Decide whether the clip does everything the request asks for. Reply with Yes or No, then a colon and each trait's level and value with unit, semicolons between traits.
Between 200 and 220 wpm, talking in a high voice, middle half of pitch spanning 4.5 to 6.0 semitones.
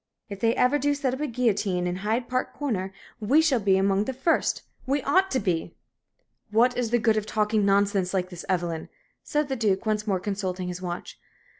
Yes: fast, 205 wpm; high, 215 Hz; average, 4.9 semitones